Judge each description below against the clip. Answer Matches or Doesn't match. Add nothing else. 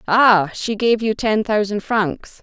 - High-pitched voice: Matches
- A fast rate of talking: Doesn't match